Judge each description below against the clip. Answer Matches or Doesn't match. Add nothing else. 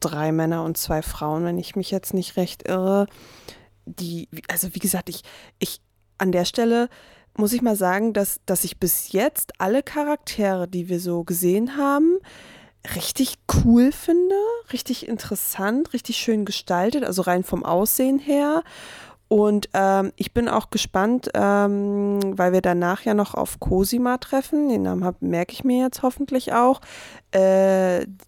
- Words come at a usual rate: Matches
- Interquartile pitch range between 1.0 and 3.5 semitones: Doesn't match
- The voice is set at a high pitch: Matches